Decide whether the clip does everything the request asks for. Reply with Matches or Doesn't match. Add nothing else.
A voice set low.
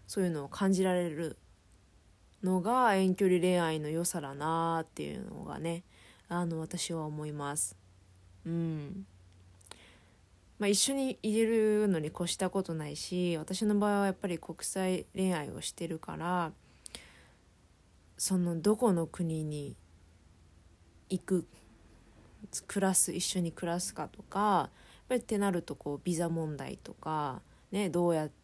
Doesn't match